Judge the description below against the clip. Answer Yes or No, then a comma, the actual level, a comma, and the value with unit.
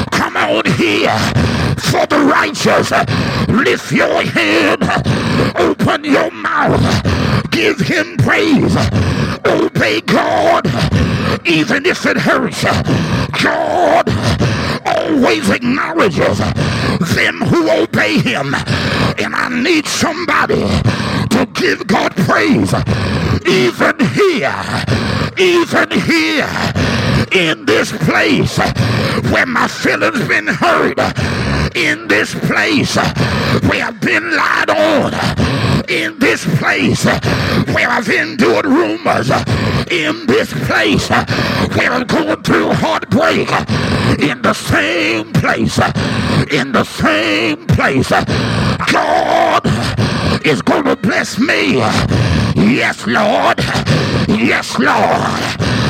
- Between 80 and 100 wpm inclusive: Yes, slow, 95 wpm